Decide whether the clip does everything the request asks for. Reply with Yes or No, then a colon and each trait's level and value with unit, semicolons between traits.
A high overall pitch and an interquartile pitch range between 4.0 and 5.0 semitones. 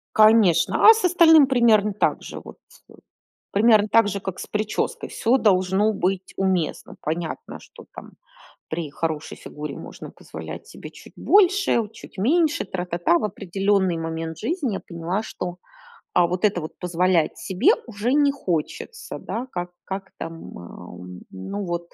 Yes: high, 195 Hz; average, 4.5 semitones